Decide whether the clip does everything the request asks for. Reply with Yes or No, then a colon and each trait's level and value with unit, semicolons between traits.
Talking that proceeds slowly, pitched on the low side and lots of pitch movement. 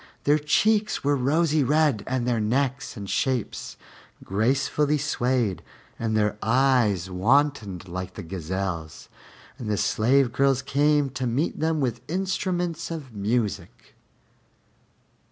Yes: slow, 120 wpm; low, 130 Hz; wide, 5.8 semitones